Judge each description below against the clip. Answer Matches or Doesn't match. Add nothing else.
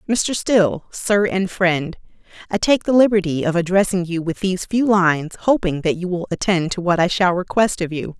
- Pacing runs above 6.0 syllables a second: Doesn't match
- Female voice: Matches